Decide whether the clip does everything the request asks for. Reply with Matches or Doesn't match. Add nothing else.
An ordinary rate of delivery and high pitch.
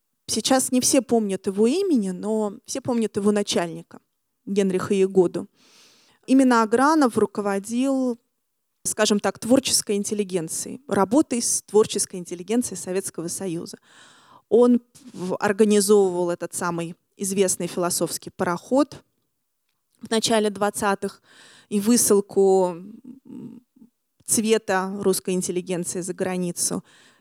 Doesn't match